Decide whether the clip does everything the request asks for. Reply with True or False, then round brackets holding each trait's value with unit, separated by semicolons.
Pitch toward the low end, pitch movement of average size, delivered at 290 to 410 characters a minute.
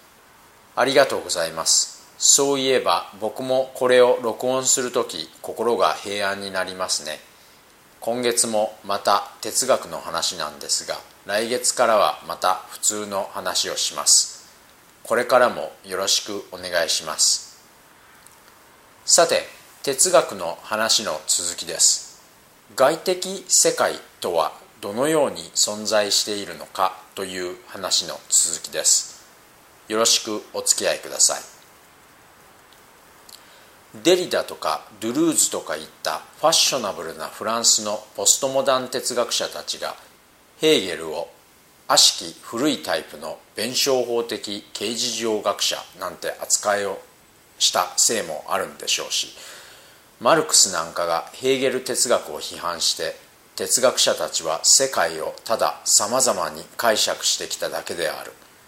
False (120 Hz; 4.5 semitones; 270 characters per minute)